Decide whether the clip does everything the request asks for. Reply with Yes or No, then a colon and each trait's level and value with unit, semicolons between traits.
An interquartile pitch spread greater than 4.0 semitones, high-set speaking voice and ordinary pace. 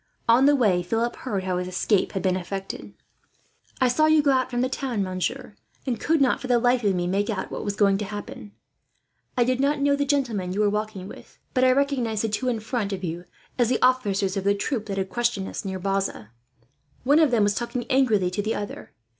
No: average, 4.7 semitones; high, 220 Hz; fast, 235 wpm